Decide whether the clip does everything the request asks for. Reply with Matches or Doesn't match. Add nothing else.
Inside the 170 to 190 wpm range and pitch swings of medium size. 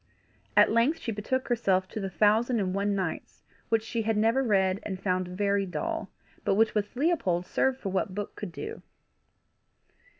Matches